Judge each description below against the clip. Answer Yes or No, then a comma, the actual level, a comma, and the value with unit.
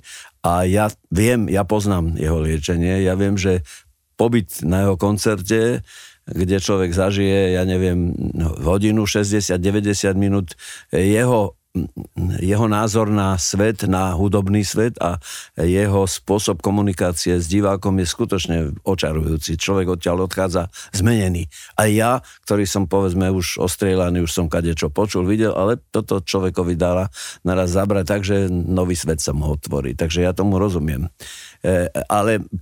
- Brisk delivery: No, average, 135 wpm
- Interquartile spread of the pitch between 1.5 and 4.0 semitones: Yes, narrow, 2.4 semitones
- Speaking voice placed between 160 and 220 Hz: No, very low, 95 Hz